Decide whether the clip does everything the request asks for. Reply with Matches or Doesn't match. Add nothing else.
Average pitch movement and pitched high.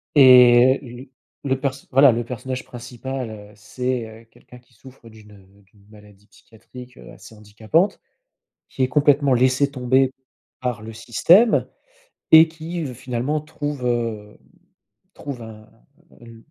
Doesn't match